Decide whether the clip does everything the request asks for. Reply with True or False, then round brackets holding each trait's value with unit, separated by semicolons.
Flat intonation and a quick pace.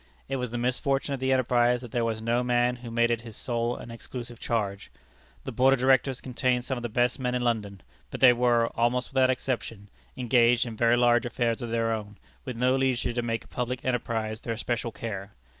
True (1.5 semitones; 225 wpm)